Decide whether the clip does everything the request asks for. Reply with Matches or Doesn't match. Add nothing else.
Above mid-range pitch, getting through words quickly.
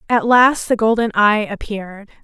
Doesn't match